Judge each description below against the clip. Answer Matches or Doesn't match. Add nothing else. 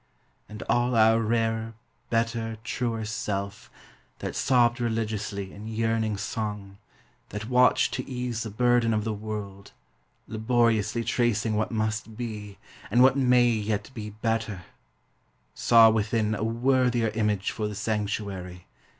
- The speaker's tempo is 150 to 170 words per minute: Doesn't match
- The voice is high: Doesn't match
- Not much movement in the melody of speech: Matches